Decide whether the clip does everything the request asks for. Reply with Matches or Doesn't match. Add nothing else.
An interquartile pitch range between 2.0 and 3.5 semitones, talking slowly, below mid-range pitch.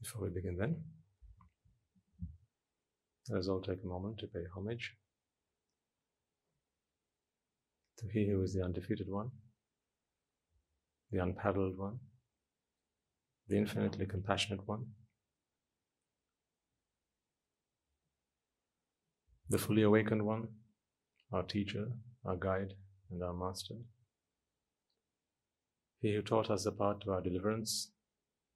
Matches